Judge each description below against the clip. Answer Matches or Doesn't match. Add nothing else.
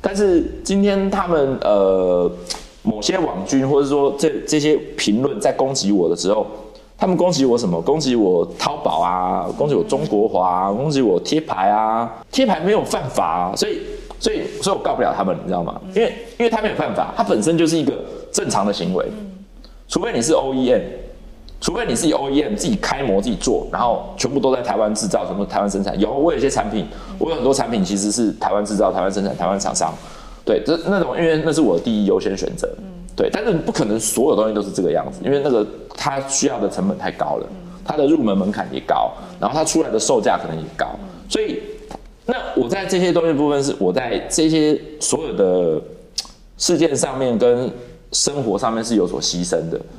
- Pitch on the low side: Doesn't match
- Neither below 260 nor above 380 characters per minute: Matches